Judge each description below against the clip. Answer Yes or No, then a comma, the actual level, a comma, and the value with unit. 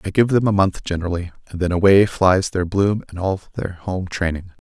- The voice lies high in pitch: No, very low, 95 Hz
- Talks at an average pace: No, fast, 220 wpm